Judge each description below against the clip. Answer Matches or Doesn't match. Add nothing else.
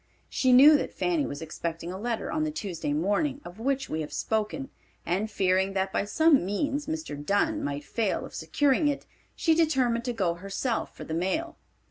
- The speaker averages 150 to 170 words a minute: Doesn't match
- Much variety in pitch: Matches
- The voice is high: Matches